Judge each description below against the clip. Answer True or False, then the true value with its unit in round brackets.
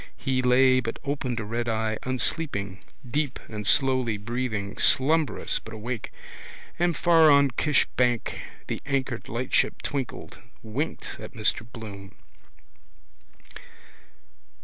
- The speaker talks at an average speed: False (115 wpm)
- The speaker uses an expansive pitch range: False (3.8 semitones)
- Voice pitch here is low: True (125 Hz)